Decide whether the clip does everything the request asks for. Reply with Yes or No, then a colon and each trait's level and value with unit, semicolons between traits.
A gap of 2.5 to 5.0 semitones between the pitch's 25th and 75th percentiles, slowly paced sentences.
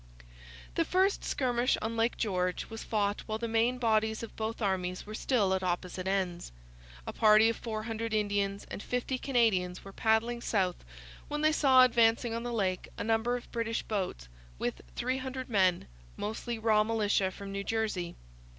No: average, 3.1 semitones; average, 170 wpm